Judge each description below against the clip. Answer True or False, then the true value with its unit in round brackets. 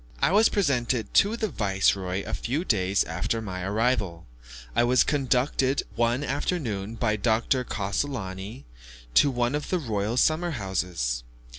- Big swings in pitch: True (6.0 semitones)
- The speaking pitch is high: False (115 Hz)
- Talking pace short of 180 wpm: True (140 wpm)